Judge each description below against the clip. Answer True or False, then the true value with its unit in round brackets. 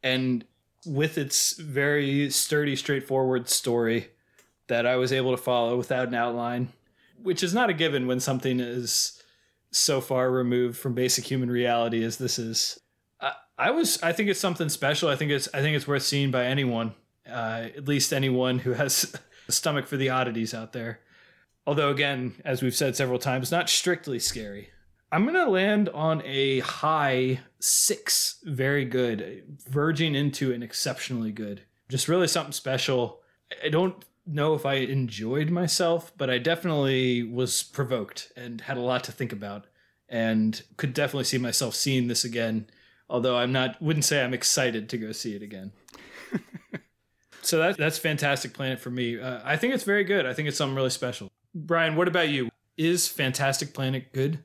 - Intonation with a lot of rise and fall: False (3.3 semitones)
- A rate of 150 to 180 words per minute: True (175 wpm)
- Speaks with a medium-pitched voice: False (130 Hz)